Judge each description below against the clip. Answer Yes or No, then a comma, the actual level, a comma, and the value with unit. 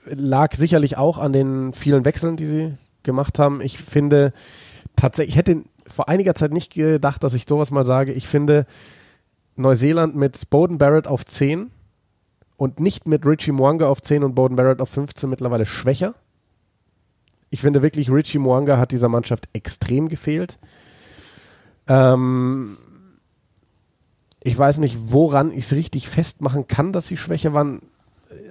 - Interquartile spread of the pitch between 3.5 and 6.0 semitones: No, average, 2.9 semitones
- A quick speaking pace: No, average, 150 wpm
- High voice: No, medium, 140 Hz